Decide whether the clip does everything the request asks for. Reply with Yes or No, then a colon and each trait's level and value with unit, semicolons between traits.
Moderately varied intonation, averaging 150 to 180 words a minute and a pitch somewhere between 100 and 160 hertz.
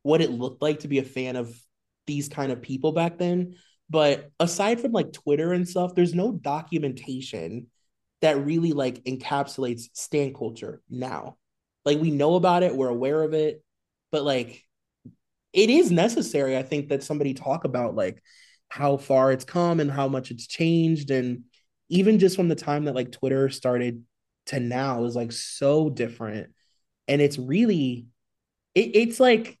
Yes: average, 4.1 semitones; average, 170 wpm; medium, 140 Hz